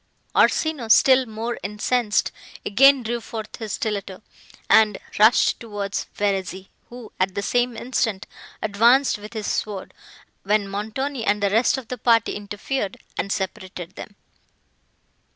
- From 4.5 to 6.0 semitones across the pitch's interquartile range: No, average, 3.1 semitones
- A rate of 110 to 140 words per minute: Yes, slow, 135 wpm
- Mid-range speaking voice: No, high, 215 Hz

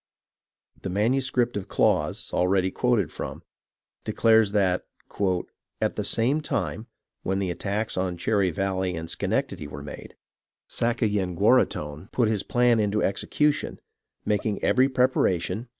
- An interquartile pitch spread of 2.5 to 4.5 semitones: Yes, average, 4.2 semitones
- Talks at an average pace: No, slow, 125 wpm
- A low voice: Yes, low, 100 Hz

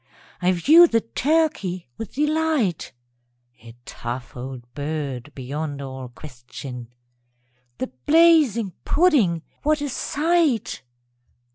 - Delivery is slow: Yes, slow, 105 wpm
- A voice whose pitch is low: No, medium, 185 Hz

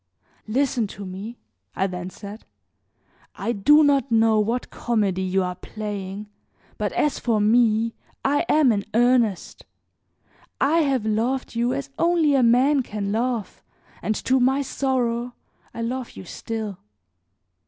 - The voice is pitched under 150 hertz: No, high, 230 Hz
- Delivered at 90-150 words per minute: Yes, average, 140 wpm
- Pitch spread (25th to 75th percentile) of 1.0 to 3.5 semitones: No, average, 3.9 semitones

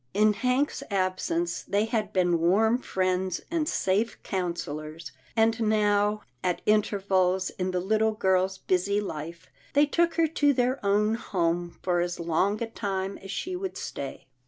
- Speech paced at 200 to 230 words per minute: No, average, 155 wpm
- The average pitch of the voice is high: Yes, high, 200 Hz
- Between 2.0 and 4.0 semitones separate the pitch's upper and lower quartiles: Yes, average, 3.5 semitones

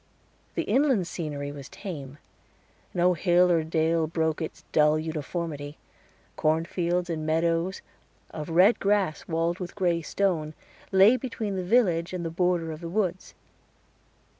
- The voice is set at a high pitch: No, medium, 170 Hz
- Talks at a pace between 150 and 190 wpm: No, average, 140 wpm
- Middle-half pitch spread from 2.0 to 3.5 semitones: Yes, narrow, 2.5 semitones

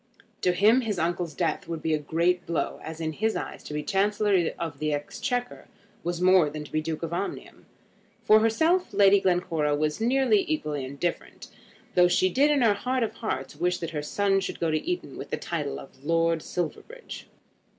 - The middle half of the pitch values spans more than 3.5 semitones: Yes, average, 5.3 semitones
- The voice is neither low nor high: Yes, medium, 175 Hz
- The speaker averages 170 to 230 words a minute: Yes, average, 200 wpm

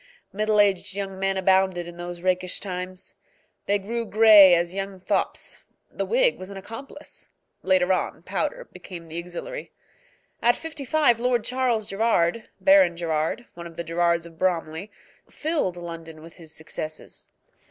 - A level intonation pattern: No, average, 4.6 semitones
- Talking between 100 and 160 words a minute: Yes, average, 155 wpm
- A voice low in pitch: No, high, 190 Hz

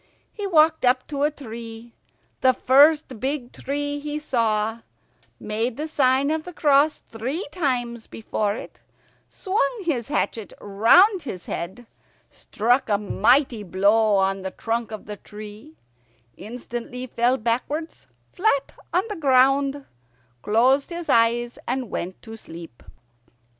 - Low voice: No, very high, 250 Hz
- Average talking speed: No, slow, 130 wpm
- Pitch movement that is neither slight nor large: Yes, average, 4.7 semitones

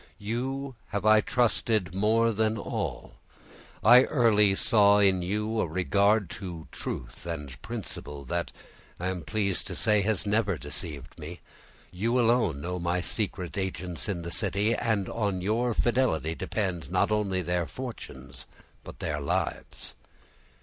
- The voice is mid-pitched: No, low, 100 Hz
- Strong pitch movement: No, average, 4.1 semitones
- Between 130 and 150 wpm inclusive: Yes, average, 140 wpm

